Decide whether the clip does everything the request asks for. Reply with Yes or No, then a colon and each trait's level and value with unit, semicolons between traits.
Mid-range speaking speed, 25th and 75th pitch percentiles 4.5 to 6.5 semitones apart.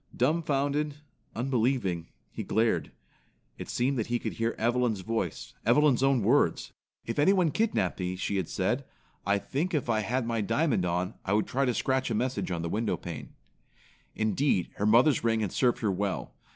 Yes: average, 180 wpm; average, 4.9 semitones